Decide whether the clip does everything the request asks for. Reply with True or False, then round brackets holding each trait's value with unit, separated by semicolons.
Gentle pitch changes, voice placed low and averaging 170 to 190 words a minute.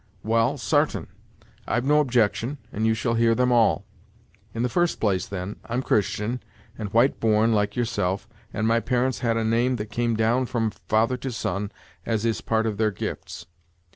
True (2.2 semitones; 115 Hz; 185 wpm)